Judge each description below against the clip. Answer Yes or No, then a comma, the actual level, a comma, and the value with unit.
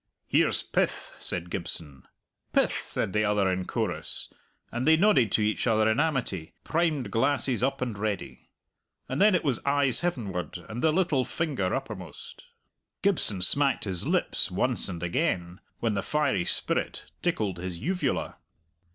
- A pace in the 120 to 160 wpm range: Yes, average, 150 wpm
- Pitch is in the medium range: No, low, 115 Hz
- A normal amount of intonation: No, wide, 7.6 semitones